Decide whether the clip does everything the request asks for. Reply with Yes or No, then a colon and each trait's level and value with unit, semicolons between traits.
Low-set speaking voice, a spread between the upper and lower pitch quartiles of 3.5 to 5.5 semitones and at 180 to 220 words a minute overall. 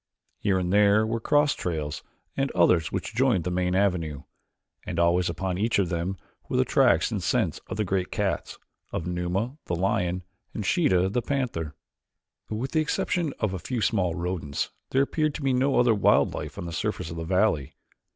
Yes: very low, 95 Hz; average, 5.1 semitones; average, 190 wpm